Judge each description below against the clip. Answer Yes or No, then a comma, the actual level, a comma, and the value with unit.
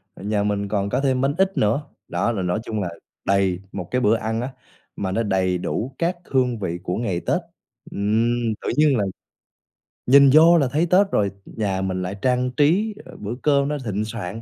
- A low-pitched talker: Yes, low, 110 Hz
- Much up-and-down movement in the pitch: Yes, wide, 5.7 semitones